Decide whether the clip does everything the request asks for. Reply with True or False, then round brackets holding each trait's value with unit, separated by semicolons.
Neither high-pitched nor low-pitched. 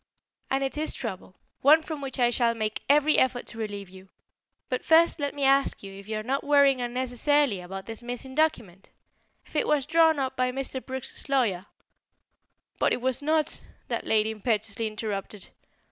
False (255 Hz)